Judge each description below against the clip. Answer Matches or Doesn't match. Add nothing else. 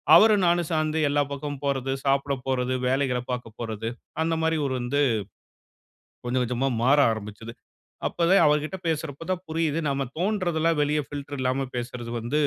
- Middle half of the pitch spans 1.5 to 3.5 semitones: Doesn't match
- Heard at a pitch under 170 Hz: Matches